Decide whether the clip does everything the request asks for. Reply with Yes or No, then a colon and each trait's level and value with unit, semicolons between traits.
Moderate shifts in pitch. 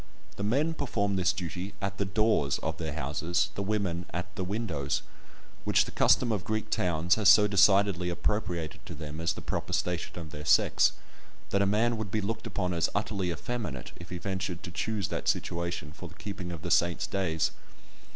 Yes: average, 3.4 semitones